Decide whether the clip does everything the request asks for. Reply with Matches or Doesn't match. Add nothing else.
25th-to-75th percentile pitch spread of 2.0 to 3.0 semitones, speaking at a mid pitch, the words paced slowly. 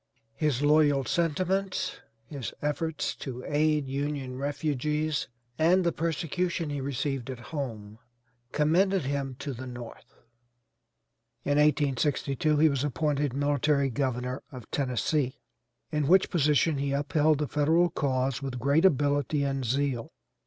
Matches